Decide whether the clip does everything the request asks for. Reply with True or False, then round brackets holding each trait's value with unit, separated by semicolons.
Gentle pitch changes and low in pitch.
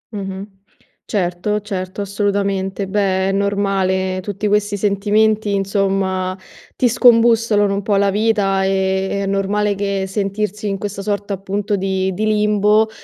False (1.3 semitones; 200 Hz)